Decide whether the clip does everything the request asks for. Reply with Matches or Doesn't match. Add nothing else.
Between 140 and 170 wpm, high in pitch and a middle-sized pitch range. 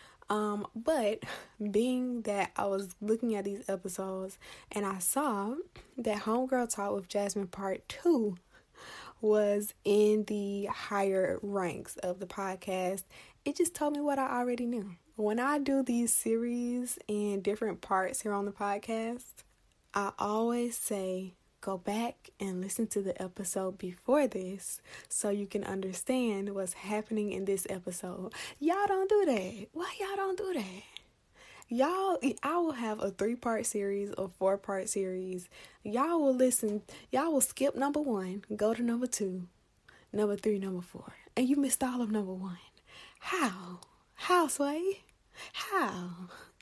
Matches